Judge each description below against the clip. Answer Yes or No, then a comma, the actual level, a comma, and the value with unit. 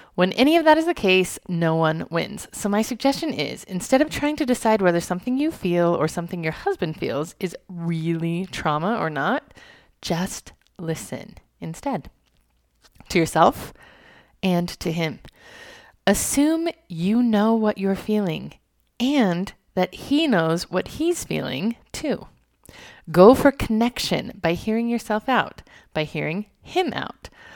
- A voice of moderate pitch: No, high, 195 Hz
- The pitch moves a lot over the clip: Yes, wide, 7.0 semitones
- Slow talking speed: No, average, 145 wpm